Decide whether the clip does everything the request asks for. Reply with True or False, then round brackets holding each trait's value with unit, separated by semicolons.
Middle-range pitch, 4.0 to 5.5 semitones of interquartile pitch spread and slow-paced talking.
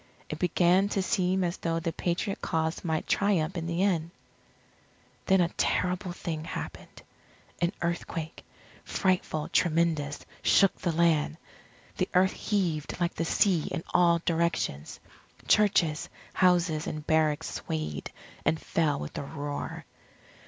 False (170 Hz; 2.6 semitones; 130 wpm)